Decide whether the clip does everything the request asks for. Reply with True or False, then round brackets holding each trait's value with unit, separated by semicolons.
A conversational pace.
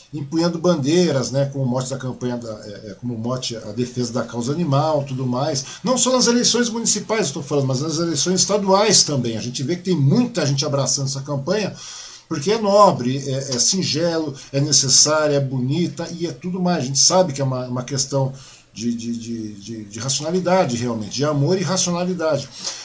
False (190 wpm)